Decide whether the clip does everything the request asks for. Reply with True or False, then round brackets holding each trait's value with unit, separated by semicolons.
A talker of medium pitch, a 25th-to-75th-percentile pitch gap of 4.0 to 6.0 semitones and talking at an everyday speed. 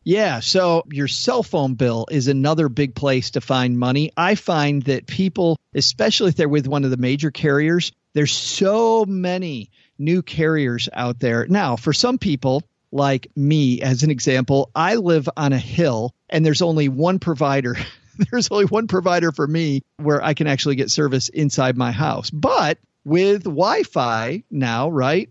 True (150 Hz; 4.6 semitones; 175 wpm)